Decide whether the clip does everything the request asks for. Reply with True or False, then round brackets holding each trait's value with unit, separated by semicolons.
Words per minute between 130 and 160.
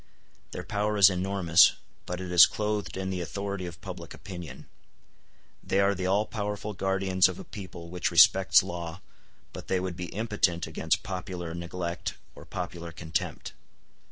True (155 wpm)